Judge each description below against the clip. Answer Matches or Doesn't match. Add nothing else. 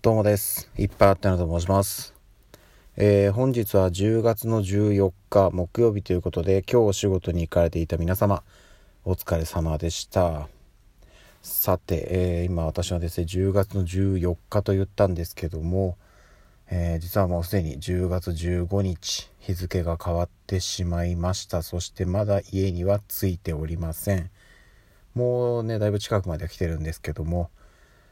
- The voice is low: Matches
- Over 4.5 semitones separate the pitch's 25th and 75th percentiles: Doesn't match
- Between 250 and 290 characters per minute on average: Matches